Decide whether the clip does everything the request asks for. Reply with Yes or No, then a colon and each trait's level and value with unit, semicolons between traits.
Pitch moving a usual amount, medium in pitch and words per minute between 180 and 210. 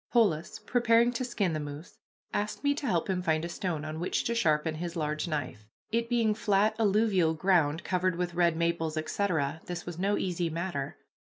Yes: average, 4.6 semitones; medium, 175 Hz; average, 190 wpm